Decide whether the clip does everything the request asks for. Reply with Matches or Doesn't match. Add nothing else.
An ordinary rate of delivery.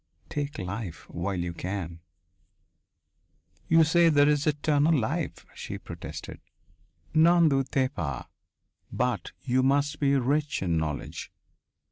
Doesn't match